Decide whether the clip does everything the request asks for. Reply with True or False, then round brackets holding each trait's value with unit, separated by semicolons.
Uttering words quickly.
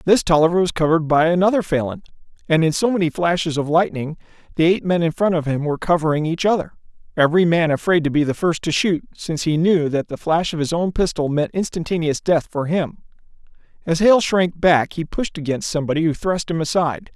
True (210 wpm)